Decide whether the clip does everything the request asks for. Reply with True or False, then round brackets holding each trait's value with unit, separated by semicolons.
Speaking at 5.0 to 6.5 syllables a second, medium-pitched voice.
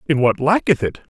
True (5.5 syllables/s; 145 Hz)